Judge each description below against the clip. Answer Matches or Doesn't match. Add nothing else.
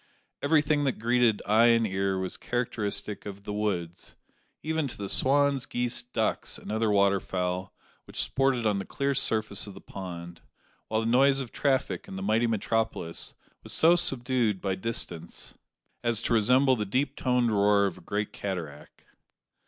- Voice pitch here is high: Doesn't match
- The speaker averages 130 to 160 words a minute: Doesn't match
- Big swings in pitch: Doesn't match